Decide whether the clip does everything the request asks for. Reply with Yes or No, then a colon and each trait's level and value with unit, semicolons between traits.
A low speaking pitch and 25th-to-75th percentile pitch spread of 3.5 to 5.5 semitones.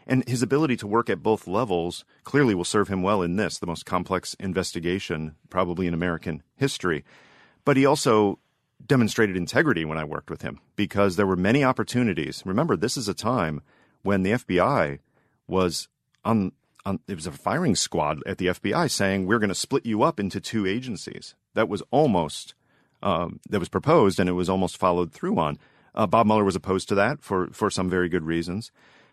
Yes: low, 100 Hz; average, 4.2 semitones